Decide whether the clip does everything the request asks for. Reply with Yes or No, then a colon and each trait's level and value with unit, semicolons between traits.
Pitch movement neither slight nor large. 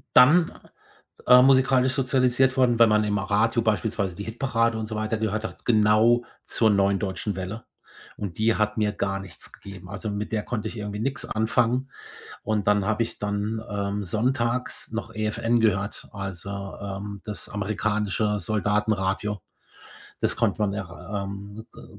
No: narrow, 2.2 semitones